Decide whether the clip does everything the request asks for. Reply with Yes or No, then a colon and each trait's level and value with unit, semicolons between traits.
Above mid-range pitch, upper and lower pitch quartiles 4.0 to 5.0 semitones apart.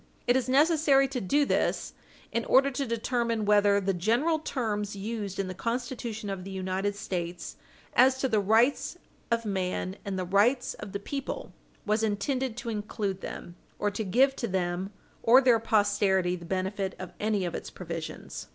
Yes: high, 210 Hz; average, 4.3 semitones